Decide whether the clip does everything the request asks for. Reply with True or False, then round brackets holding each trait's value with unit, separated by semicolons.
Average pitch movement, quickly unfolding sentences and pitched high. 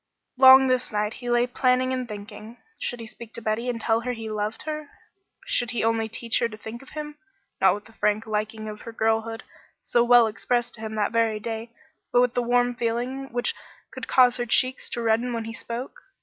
False (2.0 semitones; 220 wpm; 230 Hz)